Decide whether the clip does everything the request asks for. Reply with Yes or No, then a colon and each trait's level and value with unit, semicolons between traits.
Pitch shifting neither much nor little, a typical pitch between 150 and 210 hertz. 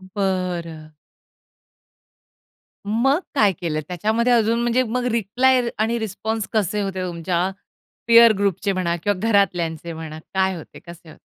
Yes: average, 4.7 semitones; high, 200 Hz